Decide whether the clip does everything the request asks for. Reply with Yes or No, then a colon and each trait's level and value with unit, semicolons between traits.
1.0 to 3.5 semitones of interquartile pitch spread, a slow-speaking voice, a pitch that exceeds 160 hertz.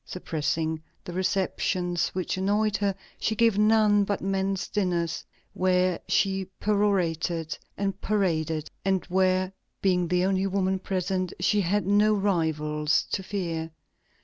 Yes: narrow, 2.4 semitones; slow, 125 wpm; medium, 185 Hz